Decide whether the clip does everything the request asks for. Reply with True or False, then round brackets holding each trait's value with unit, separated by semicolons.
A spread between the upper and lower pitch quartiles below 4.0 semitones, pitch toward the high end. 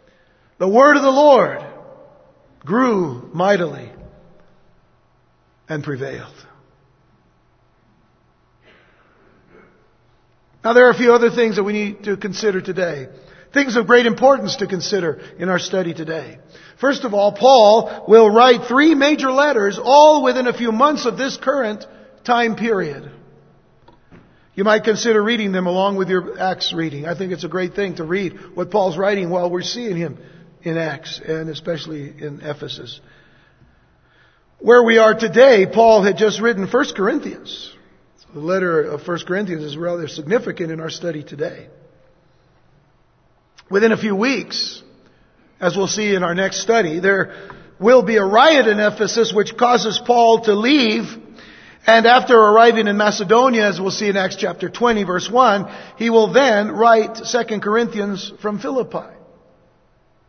False (4.8 semitones; 205 Hz)